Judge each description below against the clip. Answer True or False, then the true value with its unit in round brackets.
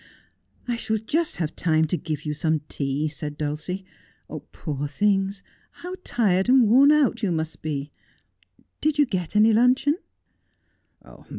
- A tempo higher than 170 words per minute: False (155 wpm)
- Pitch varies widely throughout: True (7.8 semitones)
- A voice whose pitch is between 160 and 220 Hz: True (190 Hz)